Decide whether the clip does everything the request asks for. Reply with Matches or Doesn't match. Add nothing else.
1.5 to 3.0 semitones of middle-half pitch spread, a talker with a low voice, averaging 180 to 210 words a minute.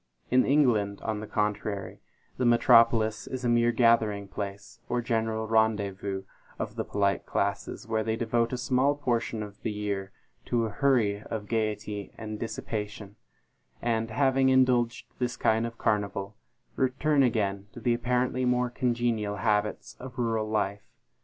Doesn't match